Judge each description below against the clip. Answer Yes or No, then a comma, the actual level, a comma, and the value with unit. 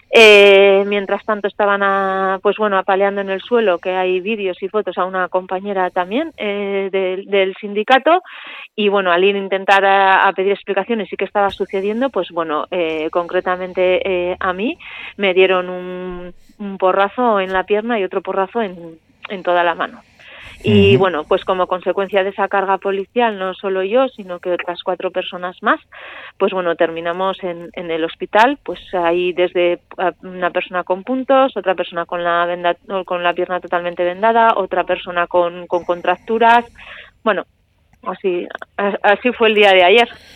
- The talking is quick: No, average, 170 wpm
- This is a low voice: No, high, 190 Hz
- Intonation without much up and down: Yes, narrow, 2.2 semitones